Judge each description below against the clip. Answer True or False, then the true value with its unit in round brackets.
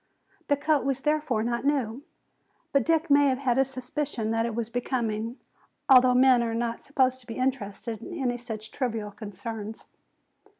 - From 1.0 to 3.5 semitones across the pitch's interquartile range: True (3.0 semitones)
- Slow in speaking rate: False (170 wpm)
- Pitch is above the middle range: True (245 Hz)